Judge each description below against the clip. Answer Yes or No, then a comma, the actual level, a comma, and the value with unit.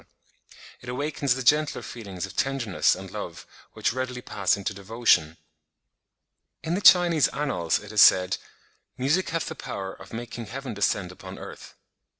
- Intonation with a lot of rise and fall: Yes, wide, 5.8 semitones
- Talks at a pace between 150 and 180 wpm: Yes, average, 155 wpm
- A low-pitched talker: Yes, low, 120 Hz